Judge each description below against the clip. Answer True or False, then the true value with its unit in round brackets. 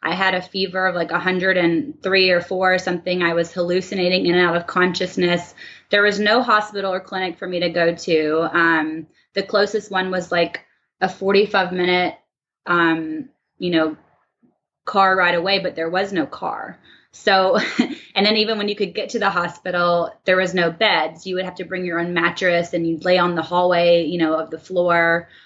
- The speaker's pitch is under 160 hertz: False (180 Hz)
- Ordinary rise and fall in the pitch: False (2.0 semitones)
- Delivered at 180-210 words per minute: True (195 wpm)